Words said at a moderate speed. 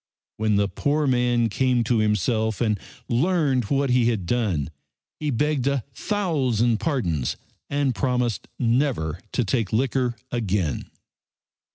No: slow, 130 wpm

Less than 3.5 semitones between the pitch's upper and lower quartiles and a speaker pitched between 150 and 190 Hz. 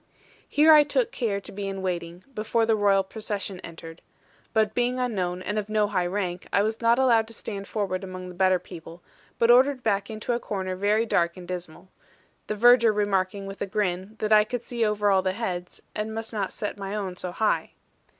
No: average, 3.1 semitones; high, 205 Hz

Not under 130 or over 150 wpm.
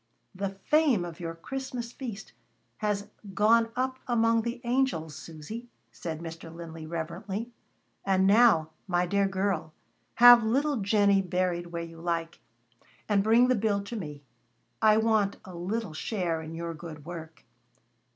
Yes: average, 145 wpm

